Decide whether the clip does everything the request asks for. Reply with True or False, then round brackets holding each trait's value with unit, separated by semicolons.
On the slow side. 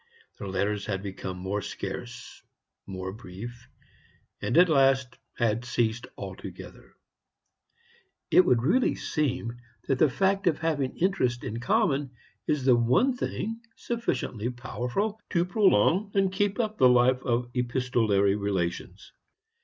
True (130 wpm)